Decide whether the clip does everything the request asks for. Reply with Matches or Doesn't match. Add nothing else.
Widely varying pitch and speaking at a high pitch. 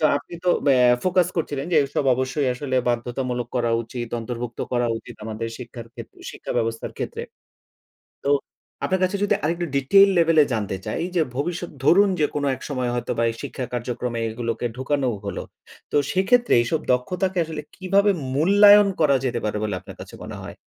Doesn't match